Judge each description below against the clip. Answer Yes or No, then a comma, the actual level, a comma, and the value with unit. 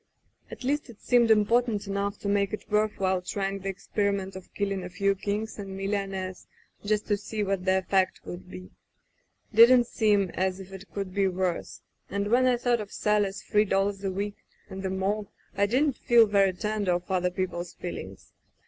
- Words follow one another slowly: No, average, 195 wpm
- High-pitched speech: Yes, high, 200 Hz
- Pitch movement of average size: No, narrow, 1.9 semitones